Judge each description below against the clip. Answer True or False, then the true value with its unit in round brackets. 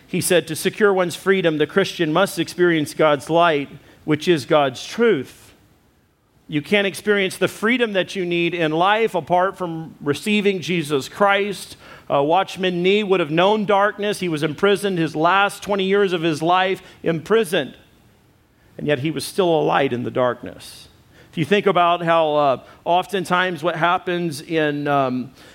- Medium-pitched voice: True (175 Hz)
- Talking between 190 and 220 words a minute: False (165 wpm)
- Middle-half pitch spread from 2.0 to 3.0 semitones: False (3.9 semitones)